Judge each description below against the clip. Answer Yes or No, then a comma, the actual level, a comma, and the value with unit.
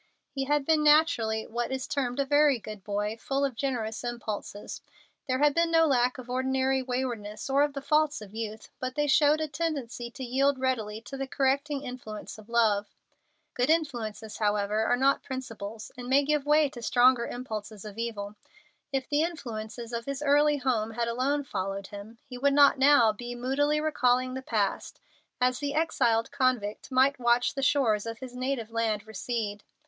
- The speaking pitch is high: Yes, very high, 255 Hz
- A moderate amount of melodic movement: Yes, average, 3.9 semitones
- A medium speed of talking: Yes, average, 185 wpm